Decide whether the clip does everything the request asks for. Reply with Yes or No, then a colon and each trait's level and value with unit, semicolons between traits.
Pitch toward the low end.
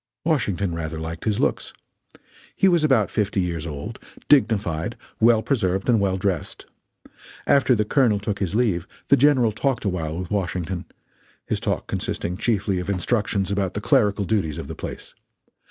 Yes: low, 100 Hz